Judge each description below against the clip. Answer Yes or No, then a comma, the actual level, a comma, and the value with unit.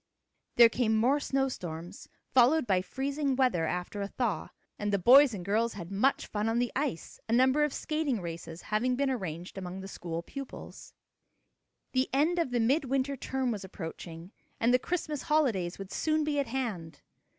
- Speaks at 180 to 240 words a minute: Yes, average, 185 wpm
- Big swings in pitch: Yes, wide, 6.2 semitones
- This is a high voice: Yes, high, 235 Hz